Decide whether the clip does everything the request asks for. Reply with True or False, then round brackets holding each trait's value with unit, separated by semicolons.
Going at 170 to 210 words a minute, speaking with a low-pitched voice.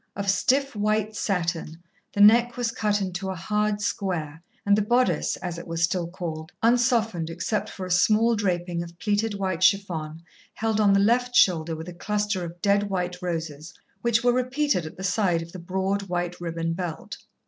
False (185 wpm; 190 Hz)